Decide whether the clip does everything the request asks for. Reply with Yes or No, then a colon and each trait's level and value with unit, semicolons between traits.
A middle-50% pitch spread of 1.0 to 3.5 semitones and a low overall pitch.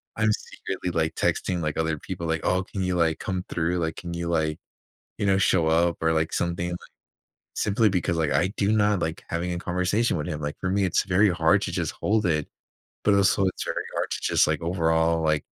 Yes: narrow, 2.6 semitones; very low, 85 Hz